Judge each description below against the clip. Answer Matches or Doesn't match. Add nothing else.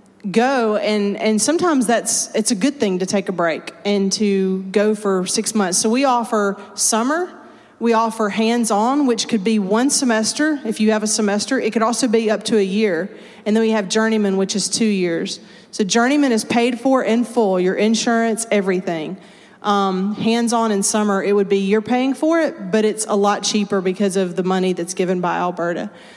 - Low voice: Doesn't match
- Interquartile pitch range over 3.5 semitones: Doesn't match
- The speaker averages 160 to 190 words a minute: Doesn't match